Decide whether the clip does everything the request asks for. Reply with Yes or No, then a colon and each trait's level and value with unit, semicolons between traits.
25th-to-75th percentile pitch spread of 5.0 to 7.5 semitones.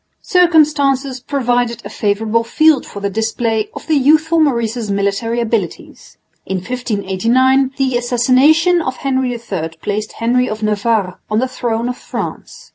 No: average, 3.7 semitones